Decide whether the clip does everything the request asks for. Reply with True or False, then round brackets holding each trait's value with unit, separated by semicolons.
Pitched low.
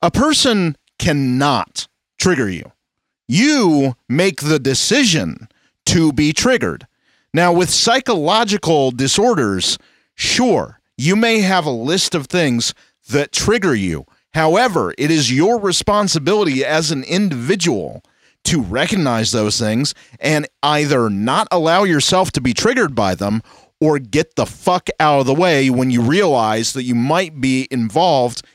False (150 Hz)